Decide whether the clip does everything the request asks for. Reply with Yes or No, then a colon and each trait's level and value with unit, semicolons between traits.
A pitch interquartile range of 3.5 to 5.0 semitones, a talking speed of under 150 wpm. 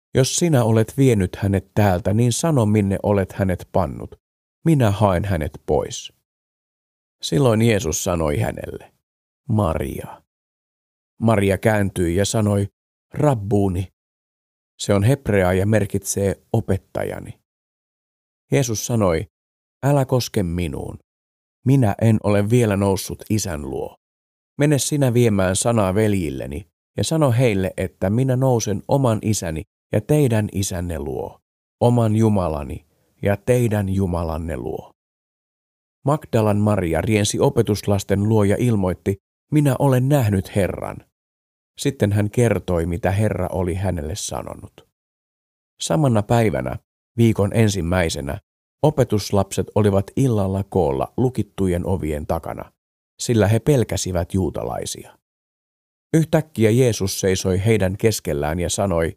Yes: average, 4.3 semitones; average, 110 wpm